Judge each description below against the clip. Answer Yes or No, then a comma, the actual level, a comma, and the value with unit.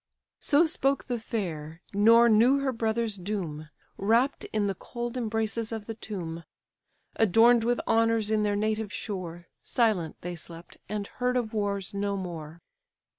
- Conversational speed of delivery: Yes, average, 150 wpm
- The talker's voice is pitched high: Yes, high, 215 Hz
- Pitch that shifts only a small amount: No, average, 3.6 semitones